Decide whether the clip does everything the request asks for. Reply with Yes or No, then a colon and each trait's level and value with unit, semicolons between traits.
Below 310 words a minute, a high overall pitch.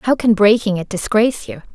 Yes: fast, 205 wpm; high, 215 Hz